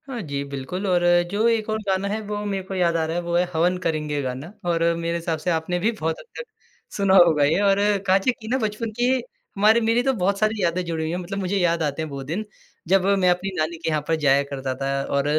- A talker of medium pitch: Yes, medium, 175 Hz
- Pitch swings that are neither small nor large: Yes, average, 4.2 semitones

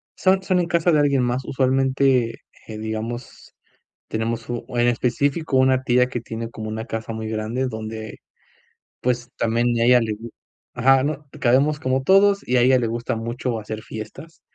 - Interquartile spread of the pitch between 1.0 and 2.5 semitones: No, average, 2.9 semitones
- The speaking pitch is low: Yes, low, 125 Hz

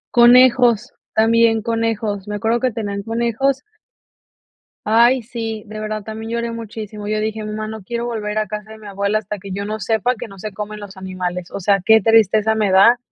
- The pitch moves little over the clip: Yes, narrow, 1.8 semitones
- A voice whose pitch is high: Yes, high, 215 Hz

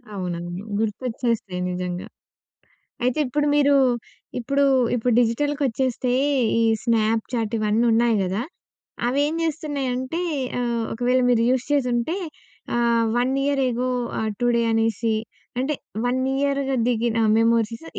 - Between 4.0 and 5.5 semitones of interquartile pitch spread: No, average, 2.8 semitones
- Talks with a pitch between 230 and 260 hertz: Yes, high, 240 Hz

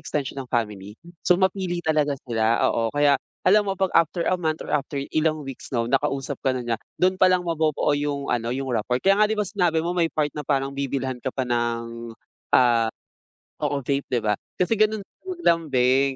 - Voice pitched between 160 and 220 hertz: No, medium, 140 Hz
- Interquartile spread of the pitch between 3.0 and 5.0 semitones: No, wide, 5.6 semitones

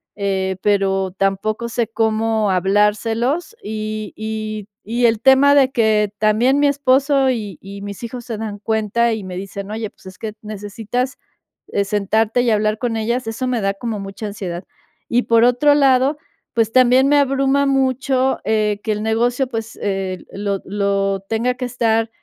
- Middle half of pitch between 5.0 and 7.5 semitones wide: No, average, 3.3 semitones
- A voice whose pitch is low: No, high, 220 Hz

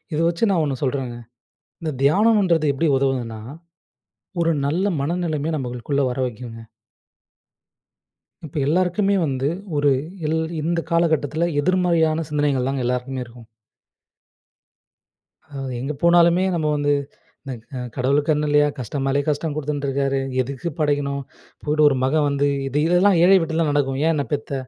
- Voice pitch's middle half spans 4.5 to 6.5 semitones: No, average, 3.4 semitones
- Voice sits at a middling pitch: Yes, medium, 145 Hz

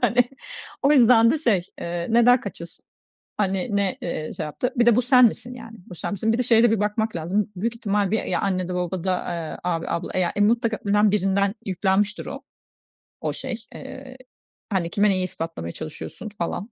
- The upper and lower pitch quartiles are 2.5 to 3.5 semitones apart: No, average, 4.1 semitones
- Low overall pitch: No, high, 205 Hz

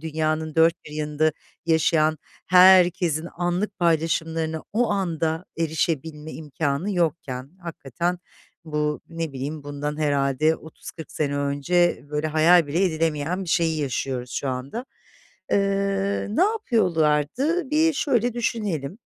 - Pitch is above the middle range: No, medium, 160 Hz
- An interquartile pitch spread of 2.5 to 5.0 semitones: Yes, average, 3.4 semitones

